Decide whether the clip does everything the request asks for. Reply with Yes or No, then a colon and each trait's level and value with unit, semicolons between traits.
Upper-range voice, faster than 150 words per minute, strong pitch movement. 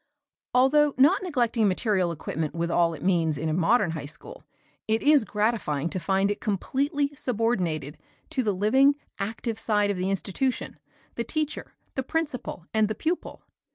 Yes: high, 215 Hz; average, 160 wpm; wide, 6.9 semitones